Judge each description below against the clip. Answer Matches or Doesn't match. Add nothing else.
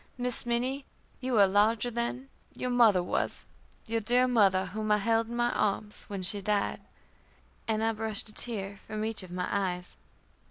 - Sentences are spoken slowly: Doesn't match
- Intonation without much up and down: Doesn't match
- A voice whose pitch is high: Matches